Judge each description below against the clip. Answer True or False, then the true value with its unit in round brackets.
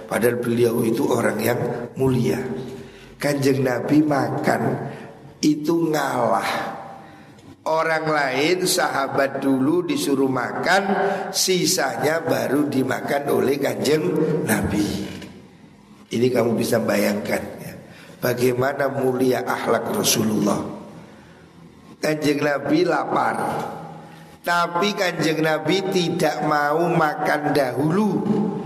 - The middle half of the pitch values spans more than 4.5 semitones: True (5.0 semitones)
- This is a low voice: False (145 Hz)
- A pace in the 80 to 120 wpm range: True (90 wpm)